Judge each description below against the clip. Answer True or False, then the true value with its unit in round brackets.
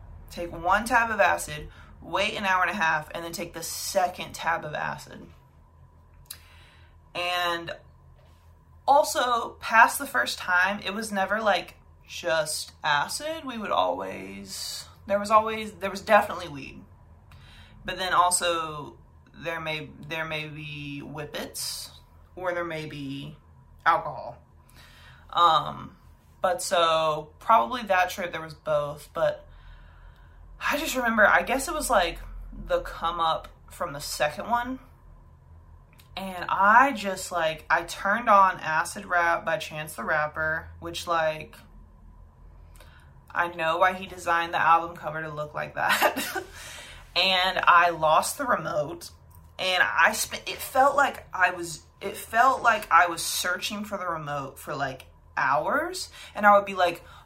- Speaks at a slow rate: False (145 wpm)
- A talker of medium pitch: True (165 Hz)